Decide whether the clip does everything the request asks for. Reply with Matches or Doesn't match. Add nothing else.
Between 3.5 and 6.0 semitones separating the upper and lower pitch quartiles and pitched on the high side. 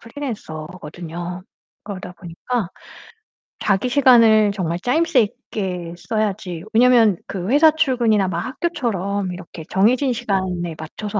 Matches